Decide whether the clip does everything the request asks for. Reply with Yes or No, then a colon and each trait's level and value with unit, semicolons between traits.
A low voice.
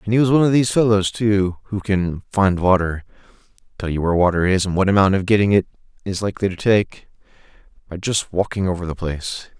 Yes: very low, 95 Hz